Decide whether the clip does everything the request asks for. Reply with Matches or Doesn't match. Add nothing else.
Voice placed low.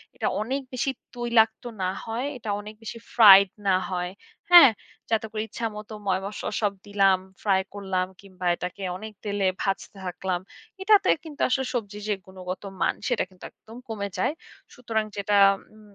Doesn't match